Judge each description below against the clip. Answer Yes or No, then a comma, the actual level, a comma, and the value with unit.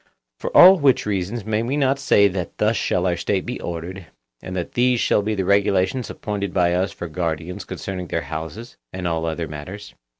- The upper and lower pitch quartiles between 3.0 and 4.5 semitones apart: Yes, average, 3.9 semitones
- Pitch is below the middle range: Yes, very low, 95 Hz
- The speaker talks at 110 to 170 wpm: No, average, 200 wpm